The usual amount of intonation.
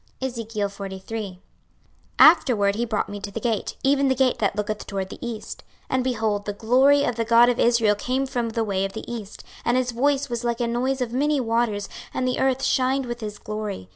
Yes: average, 3.5 semitones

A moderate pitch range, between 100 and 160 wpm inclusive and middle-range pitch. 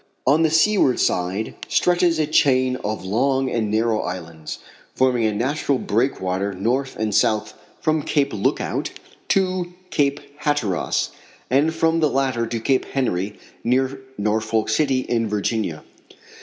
No: average, 5.0 semitones; slow, 135 wpm; low, 125 Hz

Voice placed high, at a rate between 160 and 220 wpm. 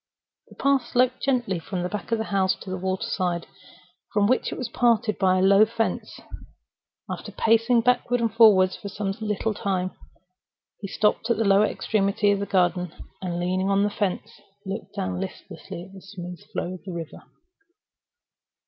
Yes: high, 200 Hz; average, 185 wpm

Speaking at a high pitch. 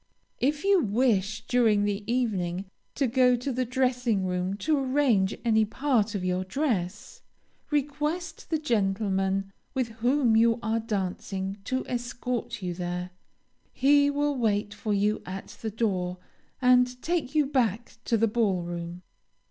Yes: high, 225 Hz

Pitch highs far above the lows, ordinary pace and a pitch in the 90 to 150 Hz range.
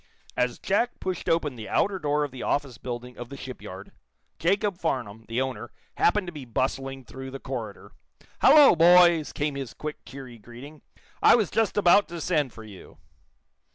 Yes: wide, 5.7 semitones; average, 175 wpm; medium, 140 Hz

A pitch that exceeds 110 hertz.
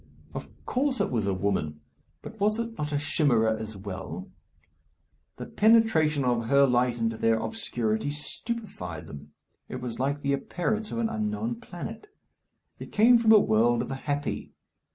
Yes: medium, 140 Hz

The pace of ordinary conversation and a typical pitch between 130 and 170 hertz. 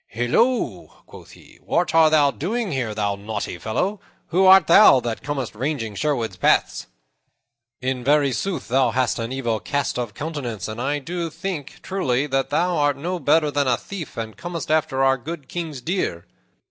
Yes: average, 175 wpm; medium, 140 Hz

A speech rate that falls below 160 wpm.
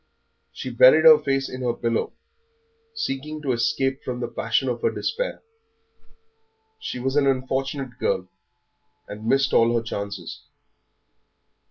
Yes: average, 140 wpm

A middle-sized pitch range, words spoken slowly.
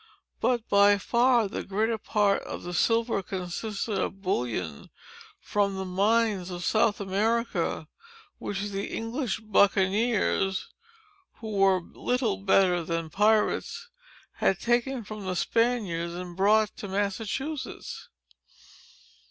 Yes: average, 3.3 semitones; slow, 110 wpm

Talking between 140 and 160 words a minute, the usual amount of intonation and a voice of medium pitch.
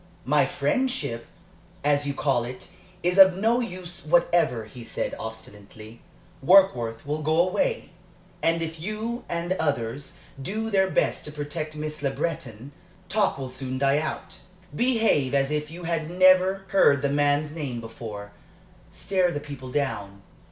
No: average, 150 wpm; wide, 5.9 semitones; medium, 150 Hz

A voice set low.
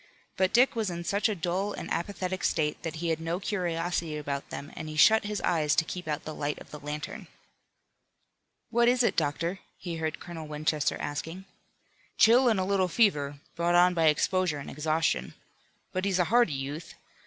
No: medium, 170 Hz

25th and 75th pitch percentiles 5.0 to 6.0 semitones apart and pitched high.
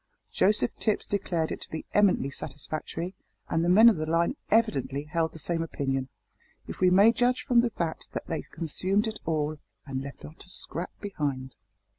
No: average, 5.3 semitones; medium, 165 Hz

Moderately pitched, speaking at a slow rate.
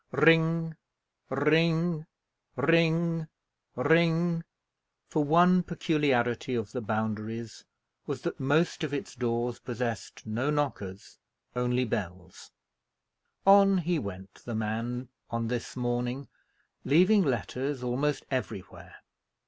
No: low, 130 Hz; slow, 100 wpm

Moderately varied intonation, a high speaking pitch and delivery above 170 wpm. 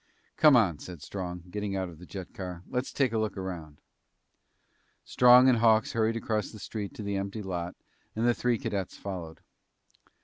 No: average, 3.9 semitones; low, 100 Hz; average, 180 wpm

